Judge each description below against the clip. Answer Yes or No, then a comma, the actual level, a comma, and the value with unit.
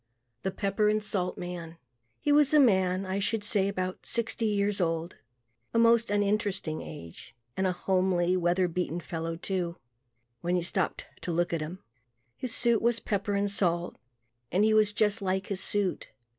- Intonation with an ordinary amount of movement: Yes, average, 3.0 semitones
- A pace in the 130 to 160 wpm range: No, average, 170 wpm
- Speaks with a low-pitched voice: No, high, 190 Hz